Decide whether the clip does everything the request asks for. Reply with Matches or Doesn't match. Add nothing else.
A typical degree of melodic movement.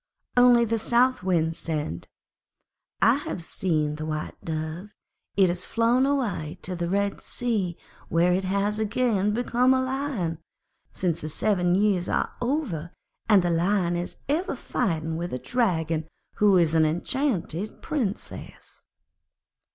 Doesn't match